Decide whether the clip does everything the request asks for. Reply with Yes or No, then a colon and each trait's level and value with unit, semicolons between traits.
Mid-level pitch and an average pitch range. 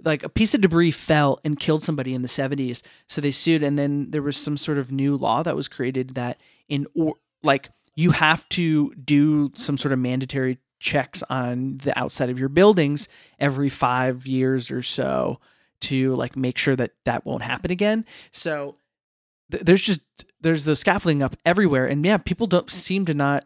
Yes: medium, 145 Hz; average, 3.5 semitones